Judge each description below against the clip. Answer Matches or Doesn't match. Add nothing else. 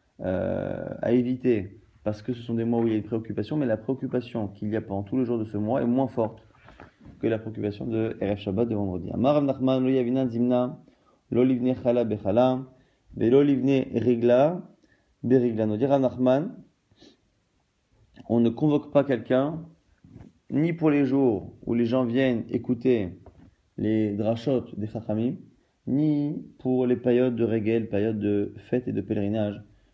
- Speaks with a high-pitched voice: Doesn't match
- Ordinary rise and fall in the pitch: Matches